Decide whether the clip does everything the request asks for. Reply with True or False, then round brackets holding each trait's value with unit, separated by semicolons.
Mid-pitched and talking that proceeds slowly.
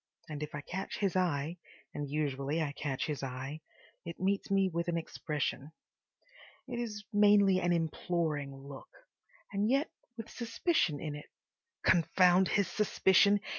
True (170 Hz; 130 wpm)